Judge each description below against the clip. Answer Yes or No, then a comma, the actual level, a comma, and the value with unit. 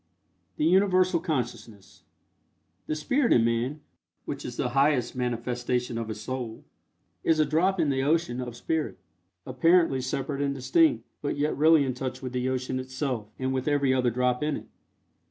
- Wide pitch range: No, average, 3.7 semitones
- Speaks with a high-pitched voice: No, low, 130 Hz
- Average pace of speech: Yes, average, 170 wpm